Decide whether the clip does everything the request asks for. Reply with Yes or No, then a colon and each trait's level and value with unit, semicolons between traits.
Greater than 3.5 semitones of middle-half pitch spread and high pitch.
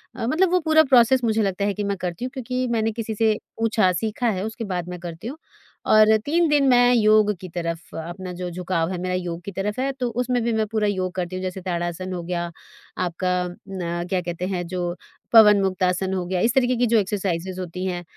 Yes: average, 4.2 semitones; high, 195 Hz